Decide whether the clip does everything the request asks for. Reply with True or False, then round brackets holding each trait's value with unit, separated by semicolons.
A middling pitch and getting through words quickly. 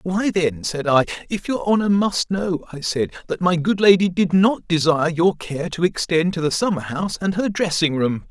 True (175 Hz; 215 wpm)